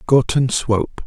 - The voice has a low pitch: Yes, low, 125 Hz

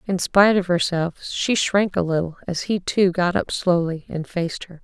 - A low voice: No, medium, 180 Hz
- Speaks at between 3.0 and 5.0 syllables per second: Yes, 4.9 syllables/s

